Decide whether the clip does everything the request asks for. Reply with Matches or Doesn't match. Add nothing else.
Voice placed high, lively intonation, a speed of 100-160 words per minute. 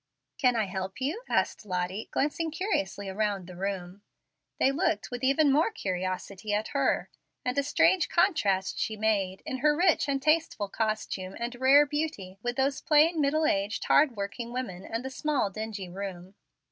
Doesn't match